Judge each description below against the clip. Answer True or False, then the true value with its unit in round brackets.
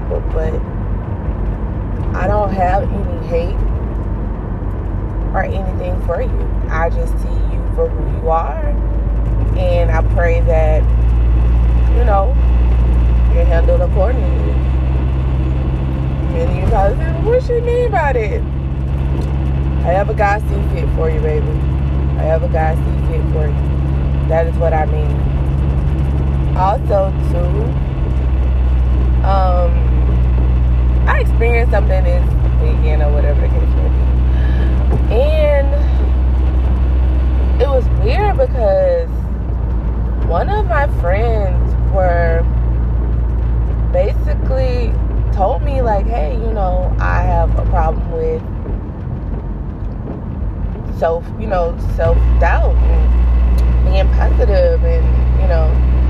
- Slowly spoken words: True (110 wpm)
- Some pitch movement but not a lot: False (2.3 semitones)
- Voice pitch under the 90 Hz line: True (65 Hz)